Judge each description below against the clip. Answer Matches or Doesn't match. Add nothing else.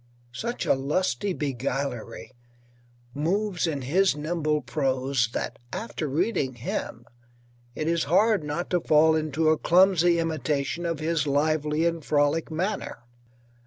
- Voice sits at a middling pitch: Matches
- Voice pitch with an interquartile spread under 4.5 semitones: Matches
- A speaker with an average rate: Doesn't match